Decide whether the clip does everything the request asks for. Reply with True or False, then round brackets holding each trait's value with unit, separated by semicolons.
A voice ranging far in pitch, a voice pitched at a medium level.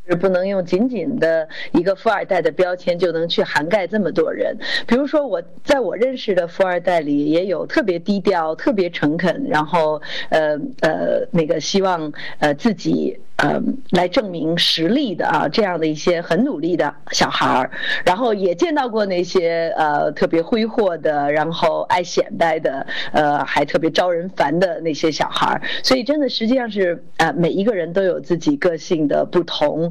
True (5.8 semitones; 180 Hz)